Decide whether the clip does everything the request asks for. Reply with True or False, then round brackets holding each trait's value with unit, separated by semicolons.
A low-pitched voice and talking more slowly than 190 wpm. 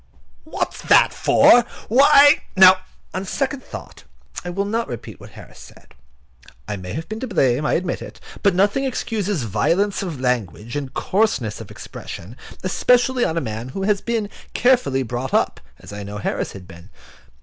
False (185 Hz; 170 wpm)